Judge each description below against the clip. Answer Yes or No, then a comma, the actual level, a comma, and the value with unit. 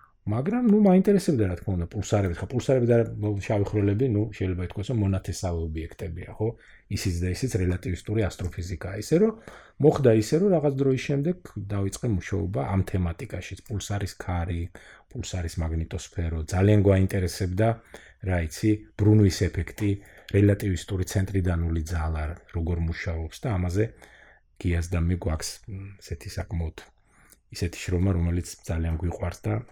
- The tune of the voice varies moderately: Yes, average, 3.5 semitones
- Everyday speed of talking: No, slow, 130 wpm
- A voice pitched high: No, low, 100 Hz